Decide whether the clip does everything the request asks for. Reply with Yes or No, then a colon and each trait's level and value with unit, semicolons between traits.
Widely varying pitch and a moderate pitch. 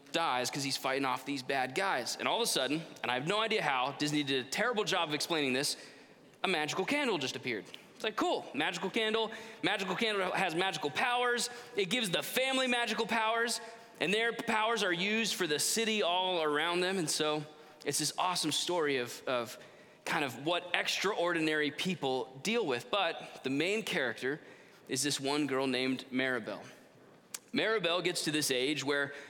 Yes: wide, 7.3 semitones; medium, 175 Hz